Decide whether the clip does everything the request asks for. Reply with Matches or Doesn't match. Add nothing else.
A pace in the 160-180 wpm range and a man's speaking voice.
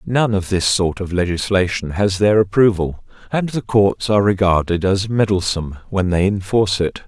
Matches